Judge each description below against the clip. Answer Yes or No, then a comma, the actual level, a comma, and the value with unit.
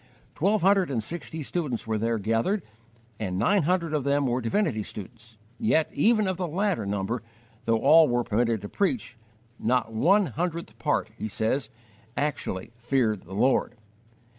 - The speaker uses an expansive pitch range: Yes, wide, 7.7 semitones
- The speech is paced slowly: No, average, 160 wpm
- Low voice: Yes, low, 130 Hz